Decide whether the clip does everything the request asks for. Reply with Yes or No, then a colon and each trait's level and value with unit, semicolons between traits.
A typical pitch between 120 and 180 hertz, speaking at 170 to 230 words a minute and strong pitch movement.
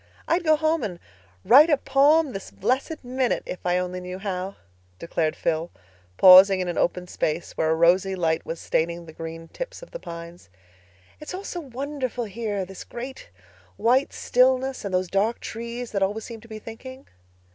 No: high, 210 Hz; average, 180 wpm; wide, 6.5 semitones